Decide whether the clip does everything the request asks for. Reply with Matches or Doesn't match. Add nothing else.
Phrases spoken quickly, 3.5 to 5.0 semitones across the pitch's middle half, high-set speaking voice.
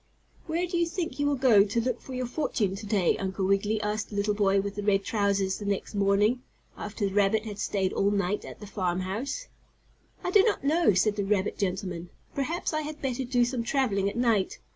Matches